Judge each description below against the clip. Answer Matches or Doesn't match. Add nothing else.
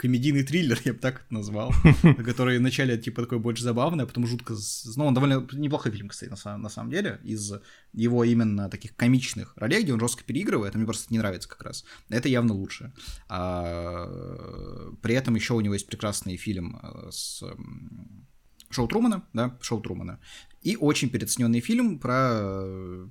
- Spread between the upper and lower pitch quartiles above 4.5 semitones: Doesn't match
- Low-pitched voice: Matches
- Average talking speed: Doesn't match